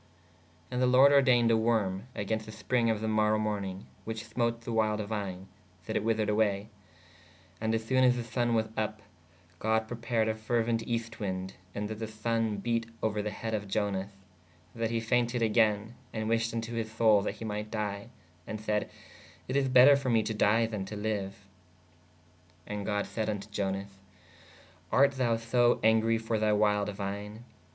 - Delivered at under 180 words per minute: No, average, 190 wpm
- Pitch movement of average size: No, narrow, 1.8 semitones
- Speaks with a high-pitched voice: No, low, 110 Hz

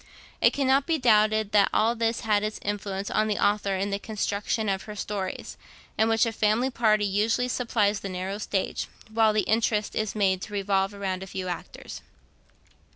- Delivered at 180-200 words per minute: Yes, average, 185 wpm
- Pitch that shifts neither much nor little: No, narrow, 1.9 semitones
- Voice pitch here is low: No, high, 210 Hz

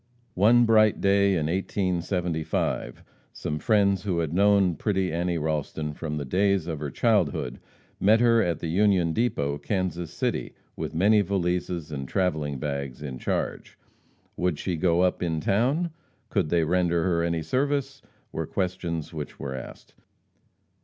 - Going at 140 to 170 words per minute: Yes, average, 150 wpm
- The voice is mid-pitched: No, very low, 90 Hz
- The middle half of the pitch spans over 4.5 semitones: No, average, 4.1 semitones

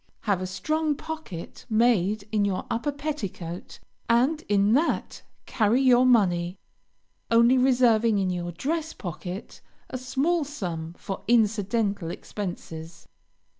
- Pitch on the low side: No, high, 220 Hz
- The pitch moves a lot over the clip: Yes, wide, 5.7 semitones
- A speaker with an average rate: No, slow, 120 wpm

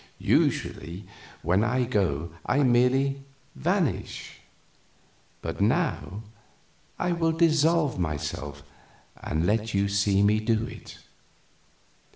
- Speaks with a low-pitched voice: Yes, low, 110 Hz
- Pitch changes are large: Yes, wide, 6.7 semitones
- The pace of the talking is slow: Yes, slow, 100 wpm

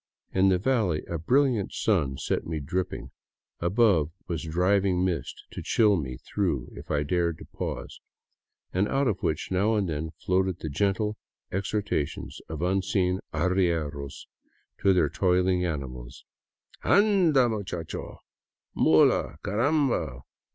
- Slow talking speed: Yes, slow, 130 wpm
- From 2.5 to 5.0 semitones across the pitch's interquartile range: Yes, average, 4.5 semitones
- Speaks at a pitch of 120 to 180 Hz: No, very low, 90 Hz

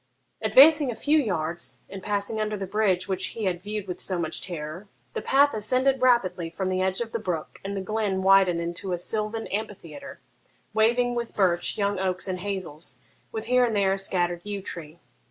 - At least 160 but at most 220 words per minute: Yes, average, 195 wpm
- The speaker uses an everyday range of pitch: Yes, average, 3.4 semitones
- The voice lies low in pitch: No, high, 195 Hz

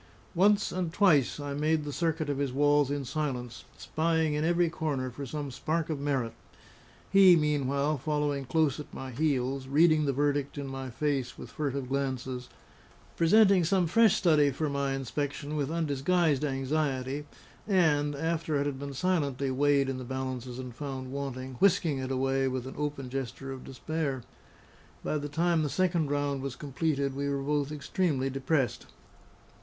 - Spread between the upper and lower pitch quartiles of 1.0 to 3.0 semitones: Yes, average, 2.7 semitones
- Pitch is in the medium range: Yes, medium, 145 Hz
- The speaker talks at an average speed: Yes, average, 165 wpm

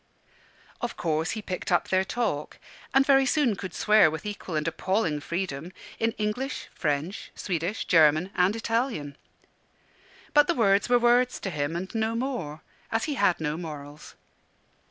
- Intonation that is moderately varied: No, wide, 6.5 semitones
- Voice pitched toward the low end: No, high, 190 Hz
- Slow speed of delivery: No, average, 155 wpm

